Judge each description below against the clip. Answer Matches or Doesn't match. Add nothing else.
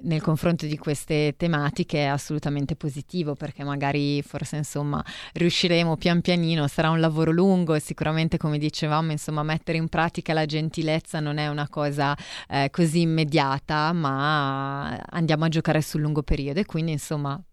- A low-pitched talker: Doesn't match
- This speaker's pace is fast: Doesn't match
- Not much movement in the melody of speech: Matches